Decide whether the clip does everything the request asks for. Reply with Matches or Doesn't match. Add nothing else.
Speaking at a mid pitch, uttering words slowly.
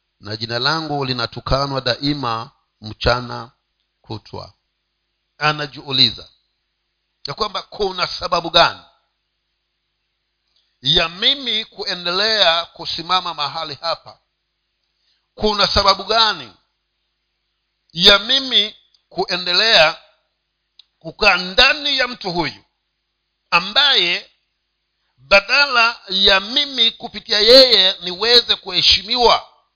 Matches